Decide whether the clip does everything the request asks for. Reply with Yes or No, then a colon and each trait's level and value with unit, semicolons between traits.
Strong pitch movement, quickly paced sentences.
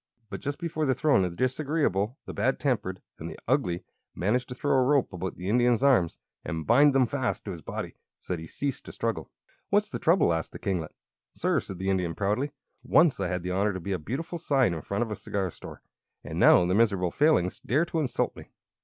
Yes: wide, 7.2 semitones; fast, 225 wpm